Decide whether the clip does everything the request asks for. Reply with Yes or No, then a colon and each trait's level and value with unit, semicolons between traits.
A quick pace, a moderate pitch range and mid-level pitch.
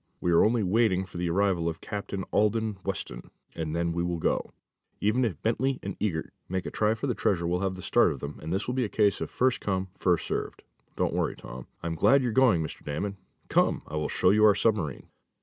No: fast, 235 wpm; average, 4.2 semitones; very low, 95 Hz